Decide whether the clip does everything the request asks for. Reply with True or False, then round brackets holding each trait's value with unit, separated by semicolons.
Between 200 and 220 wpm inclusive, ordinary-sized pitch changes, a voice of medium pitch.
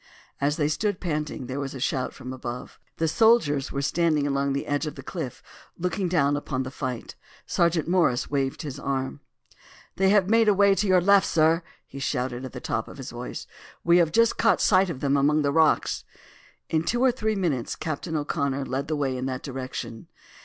True (205 wpm; 4.7 semitones; 150 Hz)